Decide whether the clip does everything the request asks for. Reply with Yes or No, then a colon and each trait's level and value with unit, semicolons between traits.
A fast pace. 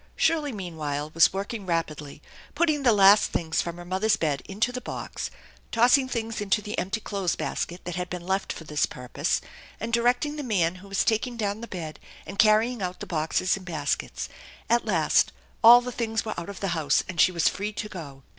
Yes: fast, 210 wpm